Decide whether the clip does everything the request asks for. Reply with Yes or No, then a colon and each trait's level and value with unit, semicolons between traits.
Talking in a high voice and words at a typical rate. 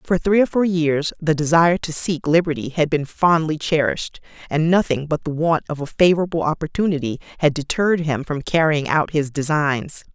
No: medium, 160 Hz; average, 185 wpm